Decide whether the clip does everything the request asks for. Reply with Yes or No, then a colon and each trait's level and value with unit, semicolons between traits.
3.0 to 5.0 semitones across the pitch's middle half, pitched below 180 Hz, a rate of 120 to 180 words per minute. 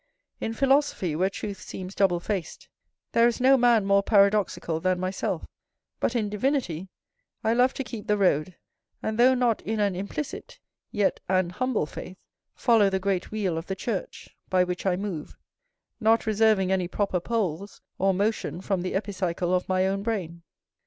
No: average, 3.3 semitones; high, 200 Hz; average, 170 wpm